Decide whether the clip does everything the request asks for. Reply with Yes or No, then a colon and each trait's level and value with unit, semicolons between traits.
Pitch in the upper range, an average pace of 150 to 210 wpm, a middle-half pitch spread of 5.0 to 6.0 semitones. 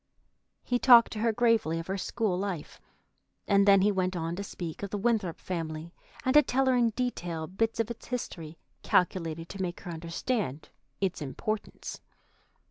Yes: high, 195 Hz; average, 175 wpm; average, 5.3 semitones